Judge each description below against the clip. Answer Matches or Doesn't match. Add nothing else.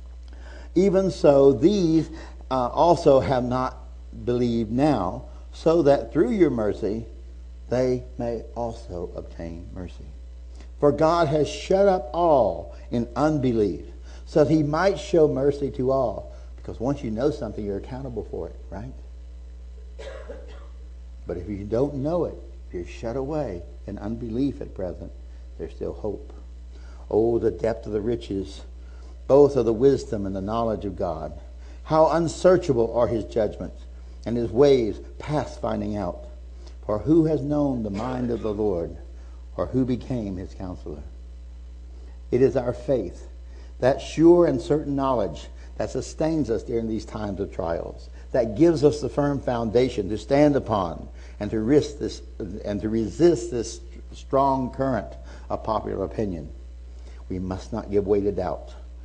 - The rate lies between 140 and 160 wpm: Matches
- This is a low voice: Matches